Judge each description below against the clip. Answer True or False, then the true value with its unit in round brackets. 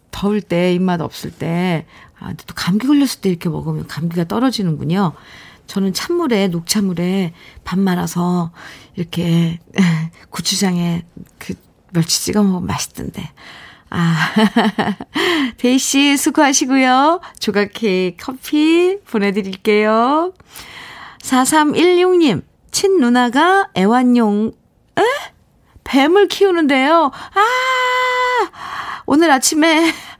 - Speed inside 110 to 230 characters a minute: True (220 characters per minute)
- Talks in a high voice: True (220 Hz)